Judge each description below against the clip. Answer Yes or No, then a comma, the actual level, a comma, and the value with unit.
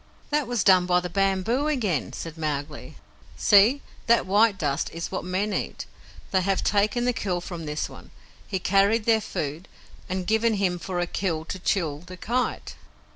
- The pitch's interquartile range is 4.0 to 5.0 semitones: No, average, 3.6 semitones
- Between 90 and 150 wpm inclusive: No, average, 180 wpm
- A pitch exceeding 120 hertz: Yes, high, 190 Hz